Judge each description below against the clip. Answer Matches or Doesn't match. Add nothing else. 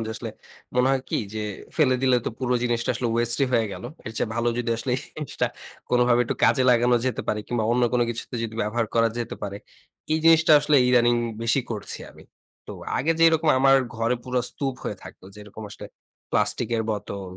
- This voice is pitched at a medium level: Doesn't match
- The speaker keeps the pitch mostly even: Matches